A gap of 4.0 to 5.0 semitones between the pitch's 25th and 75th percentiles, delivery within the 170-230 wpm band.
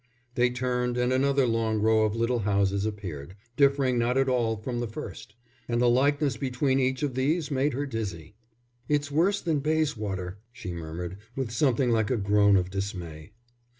Yes: average, 4.6 semitones; average, 175 wpm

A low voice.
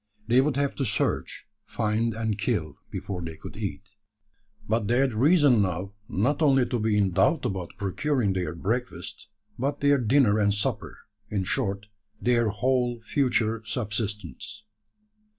Yes: low, 110 Hz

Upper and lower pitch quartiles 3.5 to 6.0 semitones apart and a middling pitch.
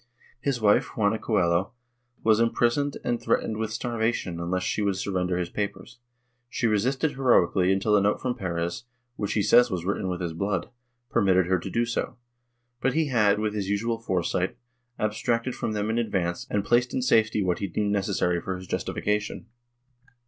No: average, 3.9 semitones; low, 105 Hz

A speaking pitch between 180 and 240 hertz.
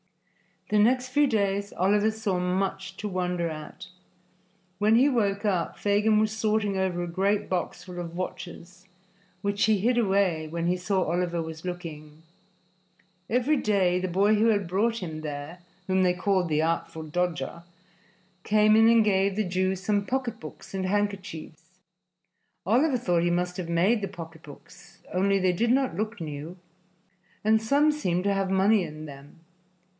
Yes: high, 190 Hz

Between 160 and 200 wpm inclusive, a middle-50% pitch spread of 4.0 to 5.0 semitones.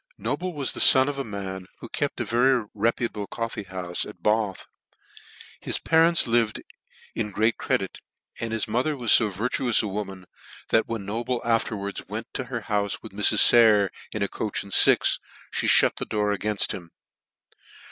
No: average, 185 wpm; average, 2.8 semitones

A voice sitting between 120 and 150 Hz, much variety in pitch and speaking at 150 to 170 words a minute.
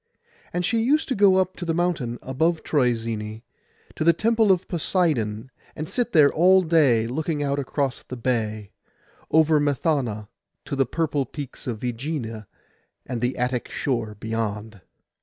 Yes: medium, 140 Hz; wide, 6.3 semitones; average, 155 wpm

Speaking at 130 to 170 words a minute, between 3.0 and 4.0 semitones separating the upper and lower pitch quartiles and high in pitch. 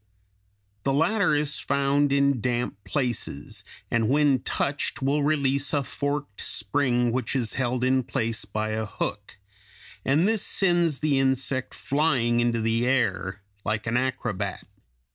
No: average, 140 wpm; average, 3.6 semitones; low, 130 Hz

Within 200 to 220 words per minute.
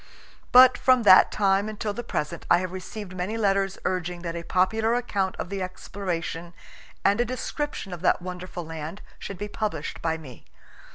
No: average, 175 wpm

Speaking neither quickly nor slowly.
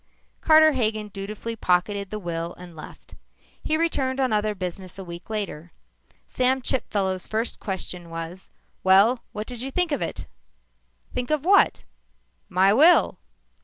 Yes: average, 145 wpm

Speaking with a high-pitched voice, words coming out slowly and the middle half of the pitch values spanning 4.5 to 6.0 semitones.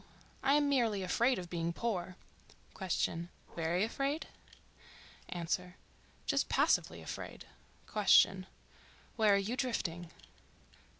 Yes: high, 195 Hz; slow, 85 wpm; average, 5.2 semitones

